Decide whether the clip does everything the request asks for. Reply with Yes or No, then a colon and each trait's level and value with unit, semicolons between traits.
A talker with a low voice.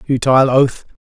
Yes: low, 130 Hz